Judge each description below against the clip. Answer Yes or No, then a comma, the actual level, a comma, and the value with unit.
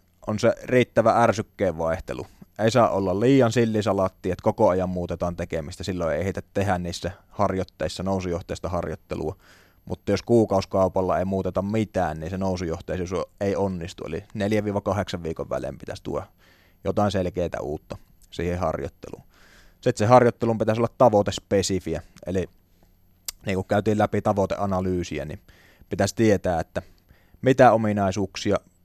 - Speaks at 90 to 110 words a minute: No, average, 130 wpm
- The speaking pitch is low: Yes, very low, 95 Hz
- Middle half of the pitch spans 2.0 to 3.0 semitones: Yes, narrow, 2.5 semitones